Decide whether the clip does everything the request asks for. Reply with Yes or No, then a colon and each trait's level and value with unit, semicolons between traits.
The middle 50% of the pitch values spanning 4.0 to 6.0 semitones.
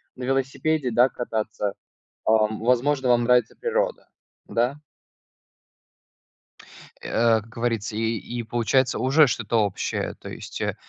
No: average, 2.9 semitones